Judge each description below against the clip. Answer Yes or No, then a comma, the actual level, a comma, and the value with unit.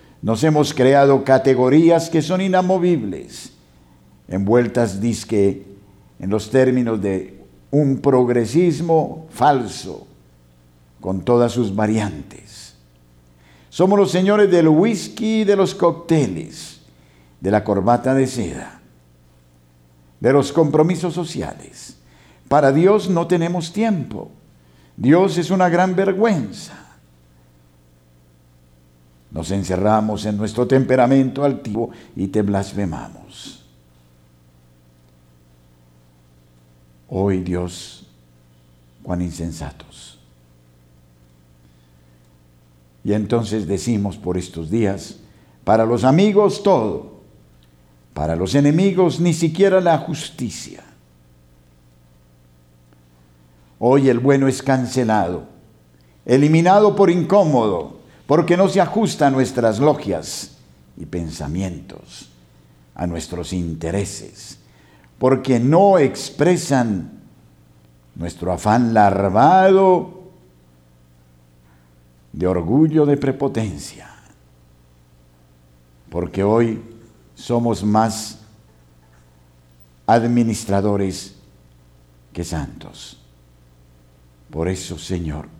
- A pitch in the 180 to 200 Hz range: No, very low, 95 Hz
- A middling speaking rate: No, slow, 80 wpm